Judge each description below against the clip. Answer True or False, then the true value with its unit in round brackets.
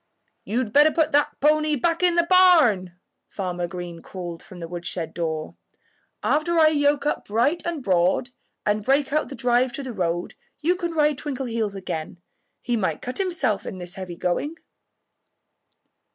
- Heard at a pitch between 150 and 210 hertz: False (245 Hz)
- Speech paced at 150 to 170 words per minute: True (165 wpm)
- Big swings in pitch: True (9.0 semitones)